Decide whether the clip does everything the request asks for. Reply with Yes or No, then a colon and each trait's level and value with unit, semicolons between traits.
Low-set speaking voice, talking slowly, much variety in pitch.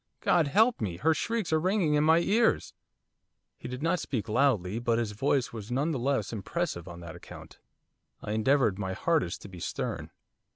No: low, 130 Hz; average, 190 wpm; wide, 7.6 semitones